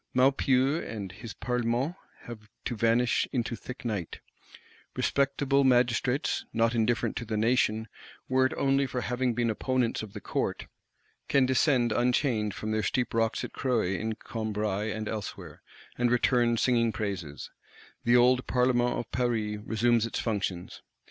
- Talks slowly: No, average, 150 wpm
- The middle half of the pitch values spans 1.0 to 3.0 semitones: Yes, narrow, 2.6 semitones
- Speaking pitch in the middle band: No, low, 120 Hz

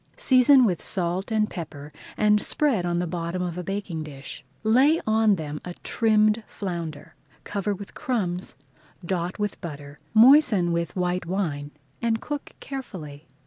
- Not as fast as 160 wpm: Yes, average, 145 wpm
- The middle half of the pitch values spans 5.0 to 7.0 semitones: No, average, 4.4 semitones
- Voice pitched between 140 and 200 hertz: Yes, medium, 185 Hz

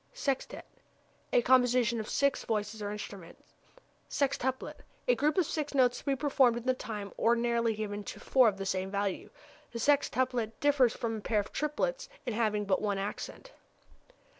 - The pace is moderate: Yes, average, 170 wpm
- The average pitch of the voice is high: Yes, high, 235 Hz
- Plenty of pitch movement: No, average, 4.4 semitones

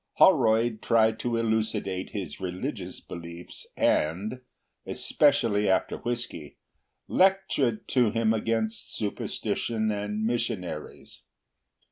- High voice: No, low, 110 Hz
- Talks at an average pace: No, slow, 80 wpm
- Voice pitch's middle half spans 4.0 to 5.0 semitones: No, average, 2.9 semitones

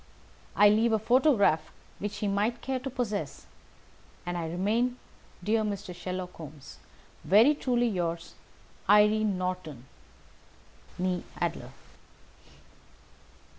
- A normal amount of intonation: Yes, average, 4.3 semitones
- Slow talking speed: Yes, slow, 105 wpm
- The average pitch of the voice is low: No, high, 205 Hz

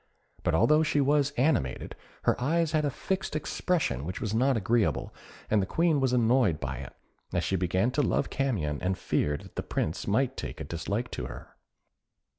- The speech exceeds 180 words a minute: Yes, average, 190 wpm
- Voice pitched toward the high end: No, low, 120 Hz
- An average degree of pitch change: No, wide, 8.7 semitones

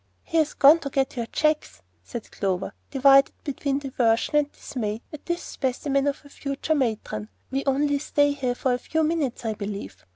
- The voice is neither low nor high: No, very high, 275 Hz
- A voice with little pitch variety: No, average, 3.9 semitones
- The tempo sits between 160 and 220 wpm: Yes, average, 175 wpm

